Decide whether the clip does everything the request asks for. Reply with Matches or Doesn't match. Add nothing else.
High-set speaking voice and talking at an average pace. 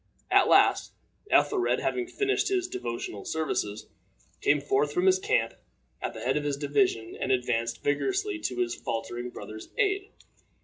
Doesn't match